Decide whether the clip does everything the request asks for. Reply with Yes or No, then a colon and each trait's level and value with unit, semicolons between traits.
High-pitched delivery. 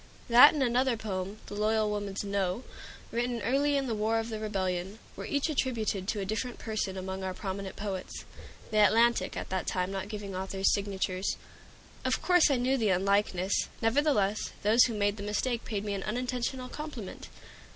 Yes: high, 210 Hz